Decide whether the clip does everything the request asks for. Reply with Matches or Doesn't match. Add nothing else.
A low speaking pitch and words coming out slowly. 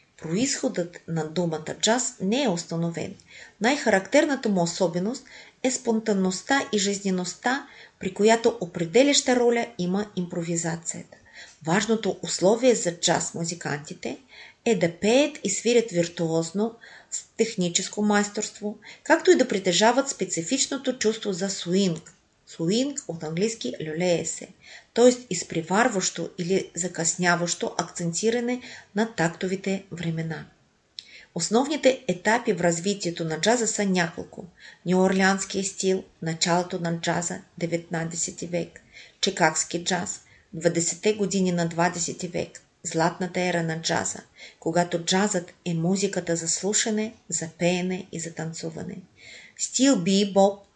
Doesn't match